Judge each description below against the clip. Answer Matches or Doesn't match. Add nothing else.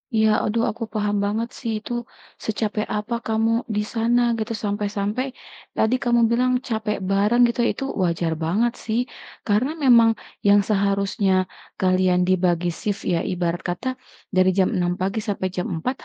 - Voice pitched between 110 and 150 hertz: Doesn't match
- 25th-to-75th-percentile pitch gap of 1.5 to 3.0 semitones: Doesn't match